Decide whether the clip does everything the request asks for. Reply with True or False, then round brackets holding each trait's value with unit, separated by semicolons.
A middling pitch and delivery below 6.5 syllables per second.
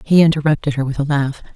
False (145 Hz; 6.7 syllables/s)